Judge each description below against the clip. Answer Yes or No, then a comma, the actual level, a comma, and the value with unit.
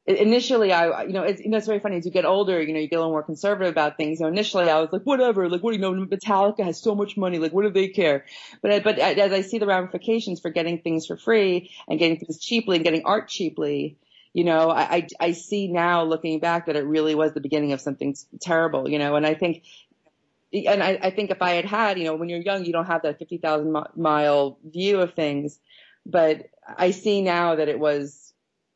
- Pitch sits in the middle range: Yes, medium, 170 Hz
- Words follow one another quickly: Yes, fast, 255 wpm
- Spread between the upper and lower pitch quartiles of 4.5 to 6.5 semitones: No, average, 3.8 semitones